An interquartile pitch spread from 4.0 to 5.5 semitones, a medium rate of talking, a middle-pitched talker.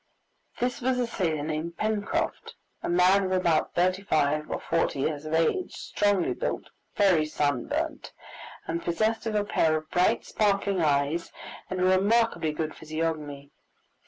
Yes: average, 4.6 semitones; average, 150 wpm; medium, 170 Hz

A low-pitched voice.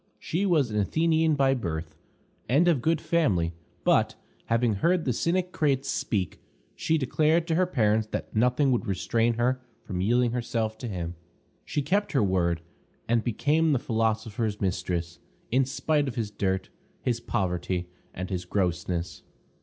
Yes: low, 115 Hz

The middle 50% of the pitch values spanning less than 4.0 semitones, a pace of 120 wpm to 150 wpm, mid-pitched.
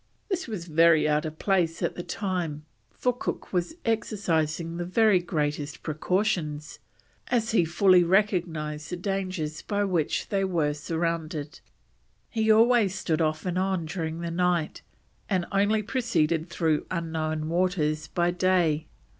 Yes: average, 3.5 semitones; average, 140 wpm; medium, 175 Hz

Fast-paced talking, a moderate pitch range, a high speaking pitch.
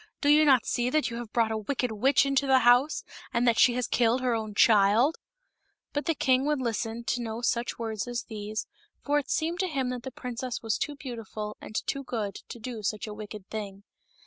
Yes: fast, 225 wpm; average, 3.2 semitones; high, 240 Hz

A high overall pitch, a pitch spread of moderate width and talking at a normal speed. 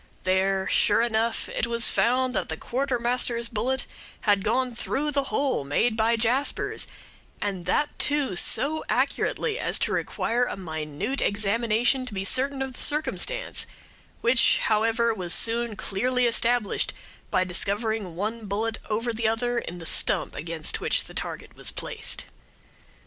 Yes: high, 230 Hz; average, 3.7 semitones; average, 150 wpm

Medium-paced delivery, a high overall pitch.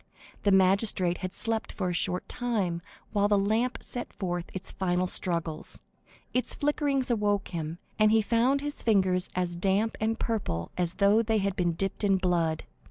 Yes: average, 170 wpm; high, 195 Hz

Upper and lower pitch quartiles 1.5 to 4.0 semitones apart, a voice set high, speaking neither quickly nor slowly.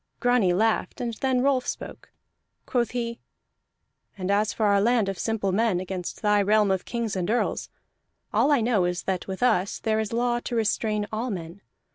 Yes: average, 3.5 semitones; high, 215 Hz; average, 185 wpm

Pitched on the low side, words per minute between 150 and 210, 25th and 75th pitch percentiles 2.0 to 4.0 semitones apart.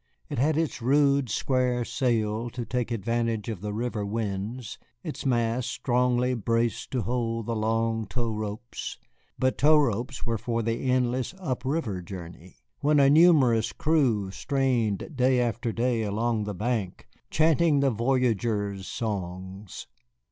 No: low, 120 Hz; average, 140 wpm; average, 3.0 semitones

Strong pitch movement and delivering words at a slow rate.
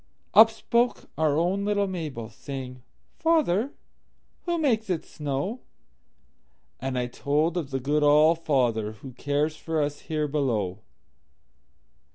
Yes: wide, 5.8 semitones; slow, 115 wpm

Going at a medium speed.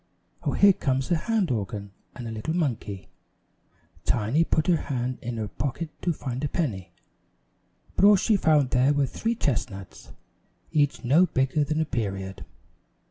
Yes: average, 160 wpm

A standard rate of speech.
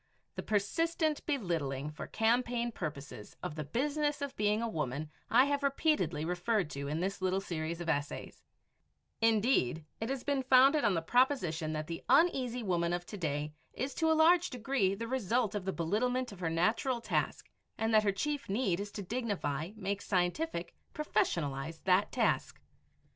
Yes: average, 170 wpm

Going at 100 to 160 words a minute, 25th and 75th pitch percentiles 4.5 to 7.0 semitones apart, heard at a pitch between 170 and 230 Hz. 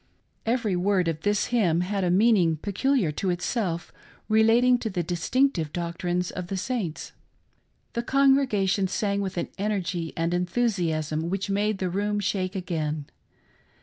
No: average, 150 wpm; average, 3.7 semitones; high, 190 Hz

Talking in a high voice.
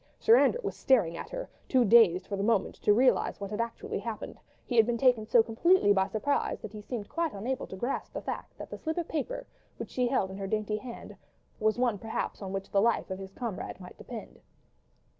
Yes: high, 225 Hz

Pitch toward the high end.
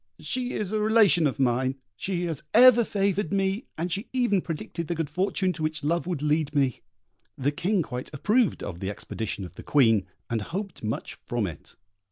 No: medium, 165 Hz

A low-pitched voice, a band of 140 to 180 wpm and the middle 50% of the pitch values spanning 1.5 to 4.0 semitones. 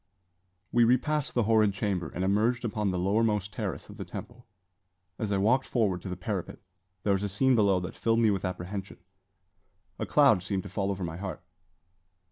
No: low, 100 Hz; average, 190 wpm; average, 3.4 semitones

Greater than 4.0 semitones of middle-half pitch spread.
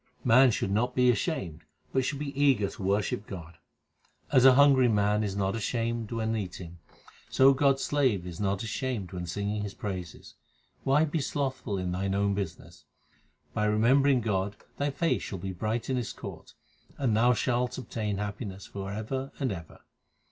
Yes: average, 5.0 semitones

